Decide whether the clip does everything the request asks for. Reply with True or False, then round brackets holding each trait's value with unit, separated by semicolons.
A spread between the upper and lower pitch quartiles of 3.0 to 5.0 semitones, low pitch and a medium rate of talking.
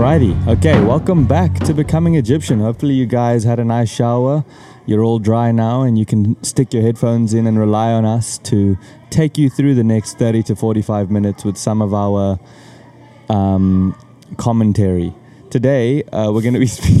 True (3.3 semitones; 115 Hz; 185 wpm)